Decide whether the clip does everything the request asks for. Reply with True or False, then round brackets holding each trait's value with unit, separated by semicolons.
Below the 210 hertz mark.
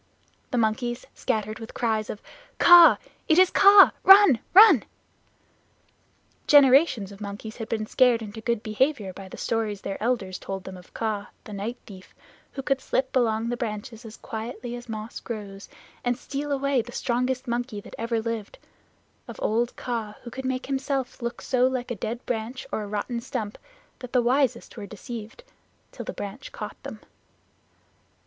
False (235 Hz)